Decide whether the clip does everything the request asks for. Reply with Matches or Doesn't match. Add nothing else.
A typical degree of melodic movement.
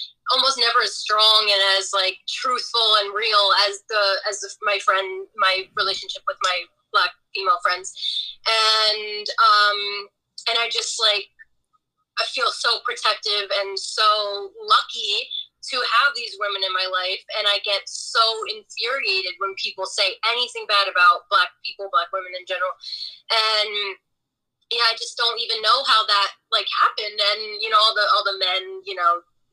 Matches